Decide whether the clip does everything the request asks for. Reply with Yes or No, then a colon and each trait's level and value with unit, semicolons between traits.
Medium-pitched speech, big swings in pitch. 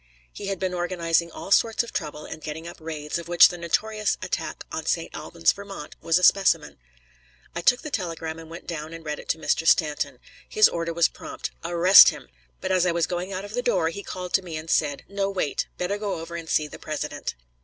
No: medium, 170 Hz; average, 3.0 semitones